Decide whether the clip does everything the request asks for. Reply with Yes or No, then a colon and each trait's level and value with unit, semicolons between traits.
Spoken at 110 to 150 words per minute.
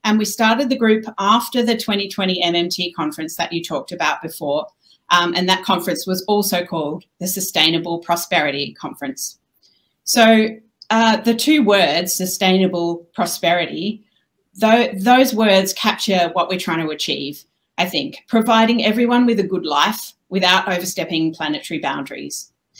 Yes: average, 140 wpm